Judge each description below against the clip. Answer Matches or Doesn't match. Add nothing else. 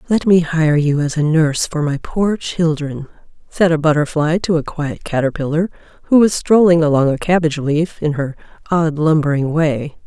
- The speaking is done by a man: Doesn't match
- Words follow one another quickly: Doesn't match